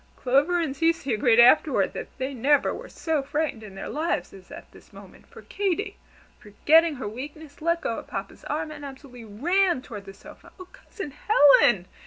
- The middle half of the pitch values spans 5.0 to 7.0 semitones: Yes, wide, 5.6 semitones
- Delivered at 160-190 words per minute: Yes, average, 185 wpm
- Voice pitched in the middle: No, very high, 280 Hz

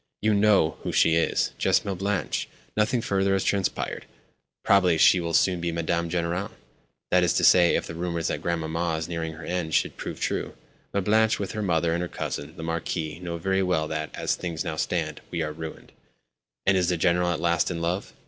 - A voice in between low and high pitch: No, very low, 85 Hz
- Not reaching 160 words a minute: No, fast, 205 wpm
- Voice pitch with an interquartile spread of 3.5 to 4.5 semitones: No, narrow, 2.6 semitones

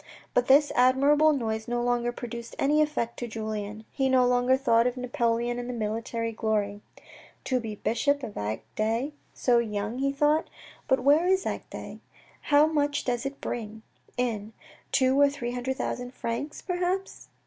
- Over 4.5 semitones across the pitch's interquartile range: No, average, 3.5 semitones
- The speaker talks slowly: No, average, 165 wpm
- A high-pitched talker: Yes, high, 245 Hz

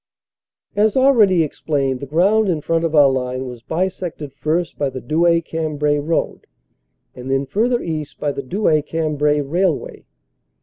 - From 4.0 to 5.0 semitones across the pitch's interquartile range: No, average, 3.6 semitones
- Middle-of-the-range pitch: Yes, medium, 155 Hz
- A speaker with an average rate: Yes, average, 150 wpm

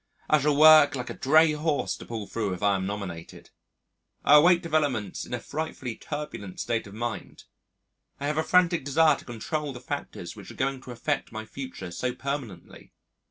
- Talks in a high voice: No, low, 135 Hz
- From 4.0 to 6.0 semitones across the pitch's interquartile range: Yes, wide, 5.6 semitones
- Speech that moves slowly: No, average, 185 wpm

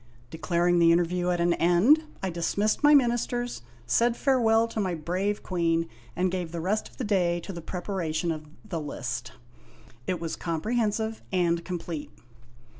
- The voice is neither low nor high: Yes, medium, 180 Hz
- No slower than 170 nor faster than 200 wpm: No, average, 160 wpm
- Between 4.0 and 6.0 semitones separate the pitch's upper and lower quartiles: Yes, average, 4.3 semitones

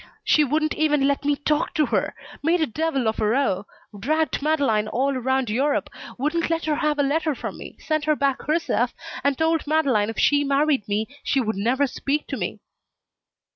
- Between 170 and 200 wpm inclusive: Yes, average, 195 wpm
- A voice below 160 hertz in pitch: No, very high, 285 Hz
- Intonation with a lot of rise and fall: No, average, 3.1 semitones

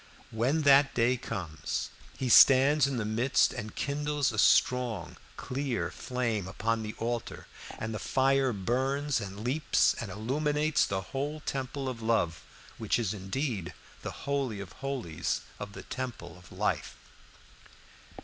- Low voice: Yes, low, 125 Hz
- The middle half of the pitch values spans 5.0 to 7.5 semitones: No, average, 4.6 semitones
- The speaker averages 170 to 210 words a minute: No, average, 140 wpm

